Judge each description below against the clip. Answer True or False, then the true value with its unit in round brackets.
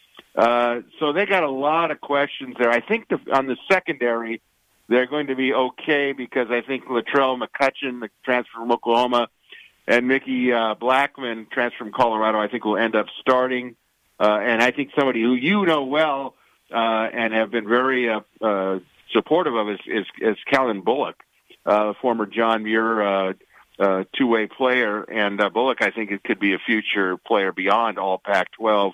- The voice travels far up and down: False (3.3 semitones)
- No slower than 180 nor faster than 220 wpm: True (185 wpm)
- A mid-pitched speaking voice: False (120 Hz)